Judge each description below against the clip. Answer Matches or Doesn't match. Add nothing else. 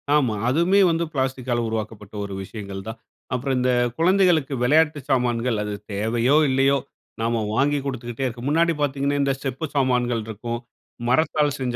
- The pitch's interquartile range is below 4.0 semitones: Matches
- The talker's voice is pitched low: Matches